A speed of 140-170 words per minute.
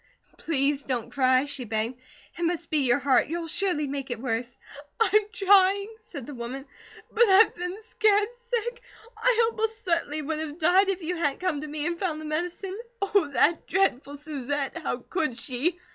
No: average, 180 wpm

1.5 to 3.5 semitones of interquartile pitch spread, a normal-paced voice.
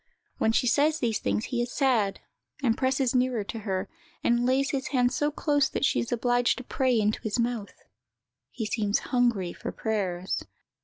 Yes: average, 3.0 semitones; average, 185 wpm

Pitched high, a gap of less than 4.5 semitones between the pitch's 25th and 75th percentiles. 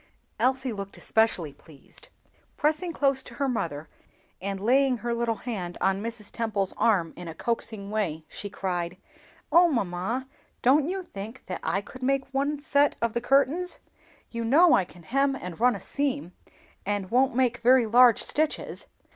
No: high, 235 Hz; wide, 5.6 semitones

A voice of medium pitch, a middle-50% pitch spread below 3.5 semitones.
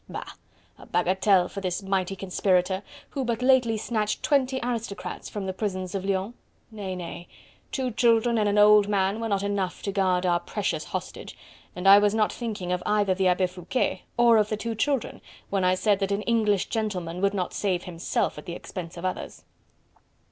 No: high, 200 Hz; average, 2.9 semitones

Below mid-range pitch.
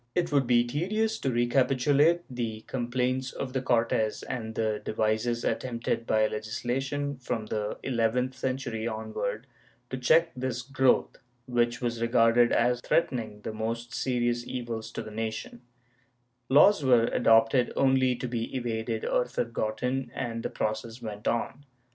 Yes: low, 120 Hz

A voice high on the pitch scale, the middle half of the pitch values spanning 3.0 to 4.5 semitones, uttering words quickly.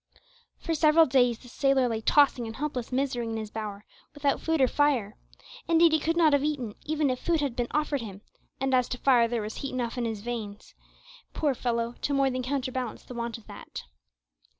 Yes: very high, 255 Hz; average, 3.7 semitones; fast, 210 wpm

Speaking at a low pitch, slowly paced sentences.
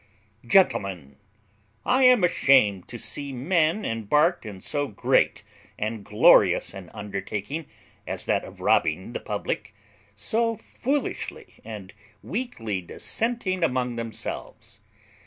Yes: low, 115 Hz; slow, 115 wpm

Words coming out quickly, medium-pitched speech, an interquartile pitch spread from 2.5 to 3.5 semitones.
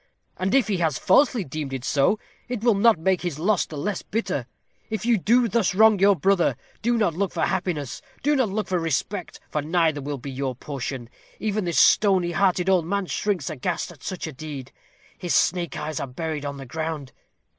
No: fast, 210 wpm; medium, 175 Hz; wide, 5.4 semitones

